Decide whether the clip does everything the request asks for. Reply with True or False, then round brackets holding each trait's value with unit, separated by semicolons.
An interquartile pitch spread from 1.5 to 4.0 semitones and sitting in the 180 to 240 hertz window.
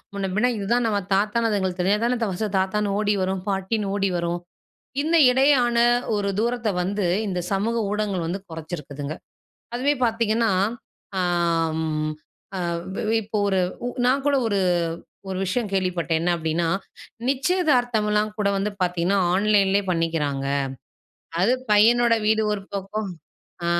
True (3.7 semitones; 205 Hz)